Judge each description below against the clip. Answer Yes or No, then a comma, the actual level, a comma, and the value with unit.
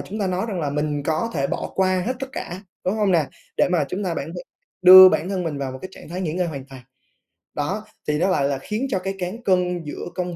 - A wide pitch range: No, average, 3.9 semitones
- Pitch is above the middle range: No, medium, 180 Hz